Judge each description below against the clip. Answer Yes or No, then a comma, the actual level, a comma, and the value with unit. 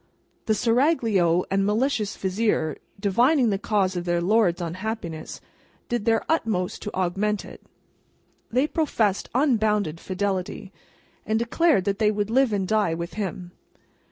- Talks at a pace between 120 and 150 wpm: Yes, slow, 135 wpm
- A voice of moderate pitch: No, high, 210 Hz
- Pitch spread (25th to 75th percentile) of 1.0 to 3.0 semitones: No, average, 3.6 semitones